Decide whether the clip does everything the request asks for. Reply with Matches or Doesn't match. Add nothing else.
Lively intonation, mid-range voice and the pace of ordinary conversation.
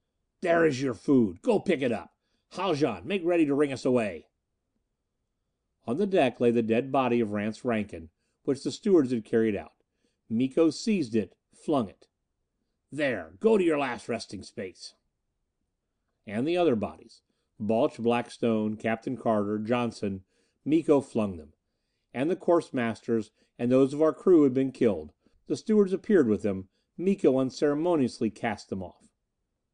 Doesn't match